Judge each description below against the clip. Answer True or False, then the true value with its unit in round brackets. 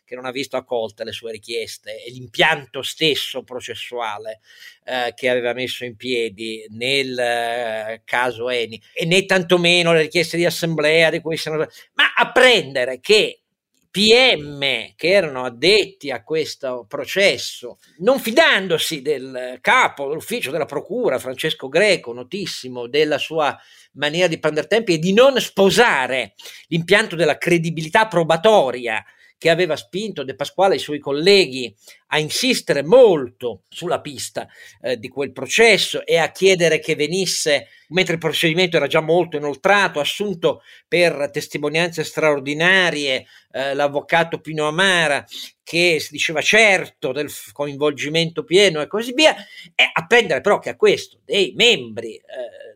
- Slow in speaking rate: False (140 wpm)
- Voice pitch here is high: False (165 Hz)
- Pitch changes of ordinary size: False (6.2 semitones)